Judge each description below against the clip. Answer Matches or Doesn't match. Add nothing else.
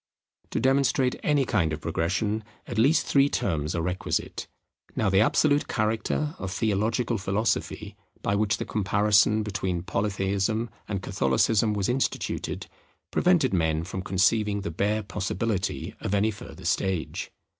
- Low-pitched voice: Matches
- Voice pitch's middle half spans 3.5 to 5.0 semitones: Doesn't match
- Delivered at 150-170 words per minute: Doesn't match